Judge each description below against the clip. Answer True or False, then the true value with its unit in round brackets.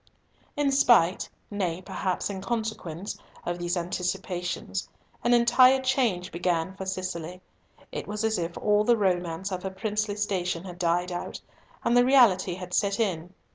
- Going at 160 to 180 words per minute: False (145 wpm)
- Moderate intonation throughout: True (3.5 semitones)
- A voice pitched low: False (190 Hz)